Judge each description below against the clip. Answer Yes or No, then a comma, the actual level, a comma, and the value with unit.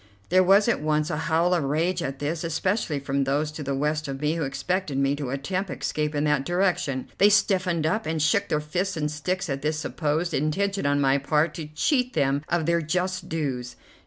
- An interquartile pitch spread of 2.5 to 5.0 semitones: Yes, average, 3.9 semitones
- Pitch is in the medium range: Yes, medium, 155 Hz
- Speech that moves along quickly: Yes, fast, 210 wpm